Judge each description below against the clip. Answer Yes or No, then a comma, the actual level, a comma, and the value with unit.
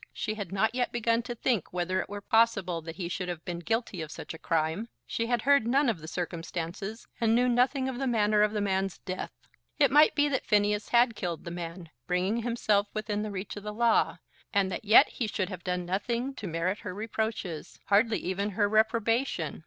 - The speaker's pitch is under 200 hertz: No, high, 210 Hz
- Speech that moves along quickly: Yes, fast, 215 wpm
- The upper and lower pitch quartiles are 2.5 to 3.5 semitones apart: No, average, 4.2 semitones